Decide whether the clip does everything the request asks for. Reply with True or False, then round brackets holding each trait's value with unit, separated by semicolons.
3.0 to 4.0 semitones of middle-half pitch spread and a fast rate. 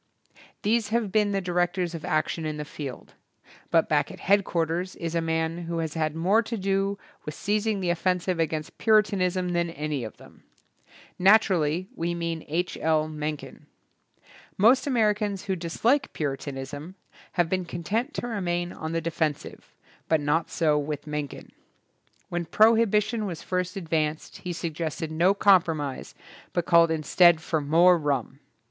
False (3.7 semitones; 155 wpm)